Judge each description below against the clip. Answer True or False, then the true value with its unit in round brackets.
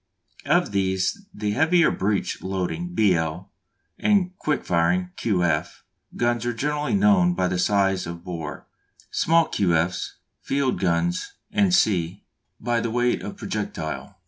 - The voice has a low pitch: True (105 Hz)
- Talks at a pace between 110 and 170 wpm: True (140 wpm)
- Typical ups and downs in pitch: False (8.7 semitones)